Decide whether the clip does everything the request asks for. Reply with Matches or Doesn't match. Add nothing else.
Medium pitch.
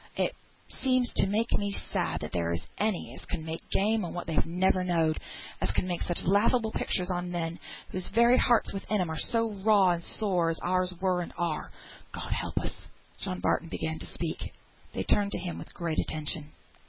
Matches